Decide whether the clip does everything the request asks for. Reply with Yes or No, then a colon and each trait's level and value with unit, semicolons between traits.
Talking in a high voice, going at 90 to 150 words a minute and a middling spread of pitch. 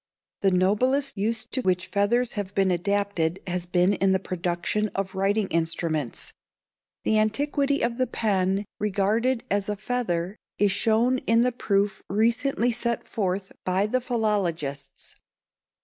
Yes: high, 205 Hz; average, 140 wpm; average, 3.7 semitones